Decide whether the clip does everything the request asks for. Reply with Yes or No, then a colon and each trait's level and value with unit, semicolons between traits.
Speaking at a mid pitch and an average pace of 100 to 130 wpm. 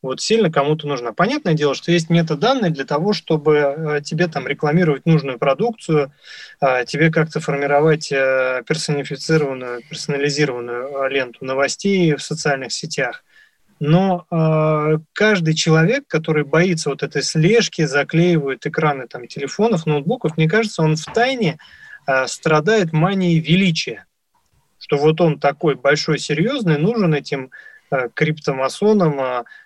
Yes: medium, 155 Hz; average, 115 wpm